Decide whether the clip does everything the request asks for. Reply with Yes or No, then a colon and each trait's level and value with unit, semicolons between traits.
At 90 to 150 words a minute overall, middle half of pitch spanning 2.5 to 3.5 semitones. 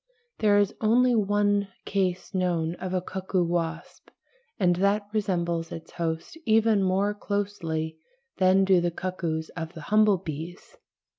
Yes: average, 140 wpm; average, 3.2 semitones